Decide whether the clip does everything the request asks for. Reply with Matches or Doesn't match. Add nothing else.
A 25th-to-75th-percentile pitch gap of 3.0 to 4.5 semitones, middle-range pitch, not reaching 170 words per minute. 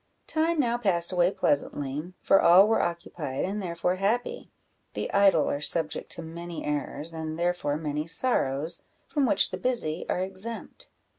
Matches